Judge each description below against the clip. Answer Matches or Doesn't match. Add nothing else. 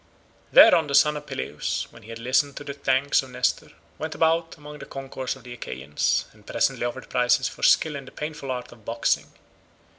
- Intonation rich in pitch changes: Doesn't match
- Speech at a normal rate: Doesn't match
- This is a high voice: Doesn't match